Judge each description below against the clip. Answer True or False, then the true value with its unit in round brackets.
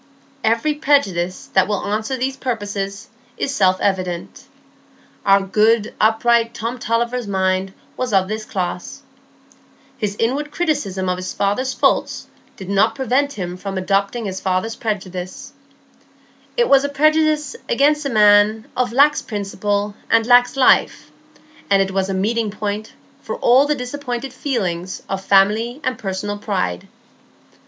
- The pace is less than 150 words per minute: True (140 wpm)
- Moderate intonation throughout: True (4.6 semitones)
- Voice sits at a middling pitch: False (215 Hz)